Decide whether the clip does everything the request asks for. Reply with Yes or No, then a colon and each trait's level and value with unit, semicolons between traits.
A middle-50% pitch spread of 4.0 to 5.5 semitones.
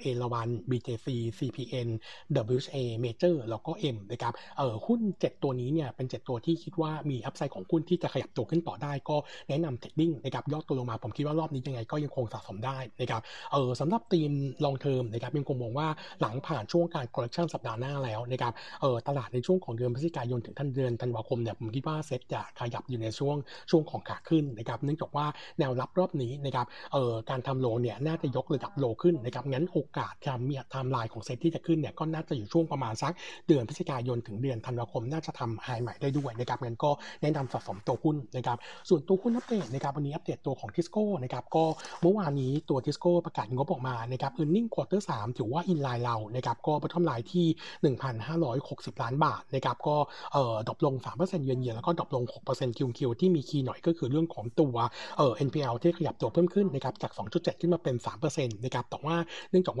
Yes: average, 4.4 semitones